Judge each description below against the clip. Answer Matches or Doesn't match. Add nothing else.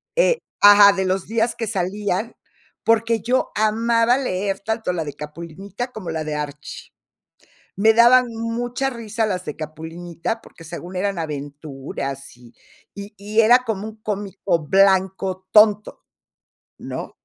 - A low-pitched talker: Doesn't match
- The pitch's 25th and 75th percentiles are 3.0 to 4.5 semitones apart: Doesn't match